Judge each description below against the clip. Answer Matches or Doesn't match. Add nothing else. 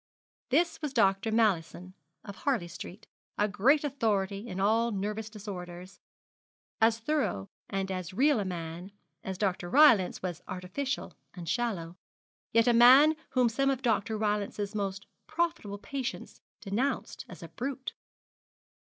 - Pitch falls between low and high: Doesn't match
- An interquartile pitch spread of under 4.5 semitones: Doesn't match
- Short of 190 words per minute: Matches